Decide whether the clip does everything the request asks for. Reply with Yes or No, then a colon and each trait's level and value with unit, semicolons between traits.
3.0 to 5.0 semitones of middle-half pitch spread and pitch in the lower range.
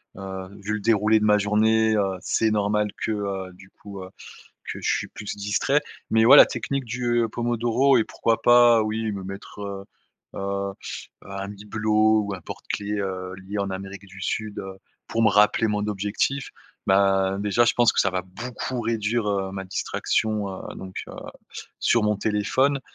No: narrow, 2.4 semitones; low, 105 Hz